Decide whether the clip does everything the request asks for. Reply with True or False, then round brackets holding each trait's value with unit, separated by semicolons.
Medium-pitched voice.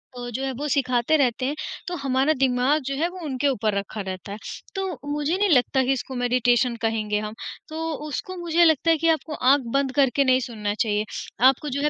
False (265 Hz)